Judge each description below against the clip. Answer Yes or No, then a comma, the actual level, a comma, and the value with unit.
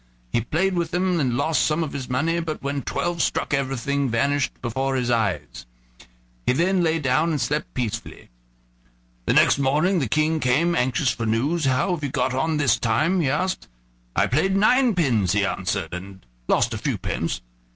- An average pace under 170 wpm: No, average, 180 wpm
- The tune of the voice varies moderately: Yes, average, 4.9 semitones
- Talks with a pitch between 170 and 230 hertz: No, medium, 140 Hz